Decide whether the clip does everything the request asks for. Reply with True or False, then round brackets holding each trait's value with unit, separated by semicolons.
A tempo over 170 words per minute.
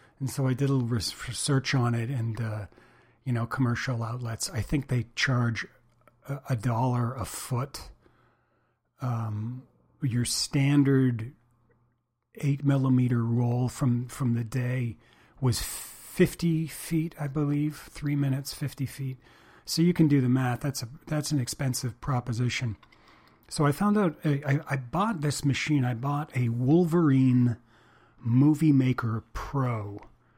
False (140 wpm)